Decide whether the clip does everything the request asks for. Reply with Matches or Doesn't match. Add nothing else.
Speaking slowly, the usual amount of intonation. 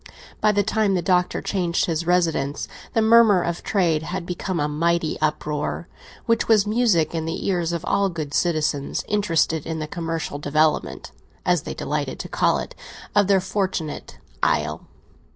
Doesn't match